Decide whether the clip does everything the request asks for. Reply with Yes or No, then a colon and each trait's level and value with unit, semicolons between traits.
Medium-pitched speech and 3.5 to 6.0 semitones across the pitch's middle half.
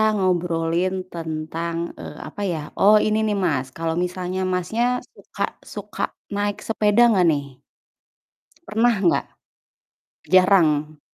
Yes: medium, 180 Hz; average, 3.9 semitones